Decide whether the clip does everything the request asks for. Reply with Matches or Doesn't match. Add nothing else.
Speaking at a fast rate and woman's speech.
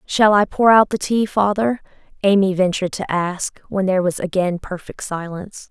Doesn't match